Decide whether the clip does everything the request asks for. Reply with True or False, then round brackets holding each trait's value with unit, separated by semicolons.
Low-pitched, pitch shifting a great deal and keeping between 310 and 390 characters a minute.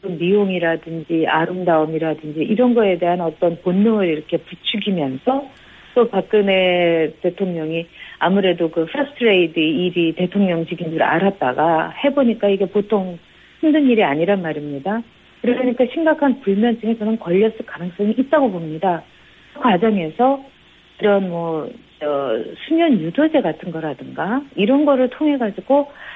False (195 Hz; 6.4 semitones; 315 characters per minute)